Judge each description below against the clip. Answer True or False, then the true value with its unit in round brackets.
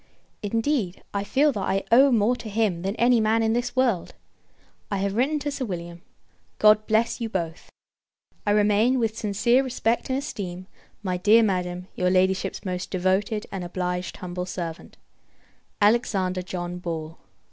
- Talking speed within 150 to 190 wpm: True (160 wpm)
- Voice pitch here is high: True (205 Hz)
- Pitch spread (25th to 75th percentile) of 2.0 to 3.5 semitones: False (4.1 semitones)